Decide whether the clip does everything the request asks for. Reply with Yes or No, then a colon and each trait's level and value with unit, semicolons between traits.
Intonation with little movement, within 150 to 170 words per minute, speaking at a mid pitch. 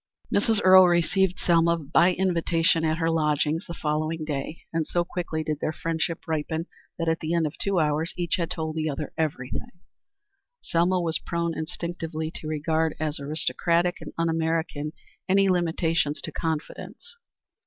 Yes: narrow, 1.7 semitones; average, 160 wpm; medium, 165 Hz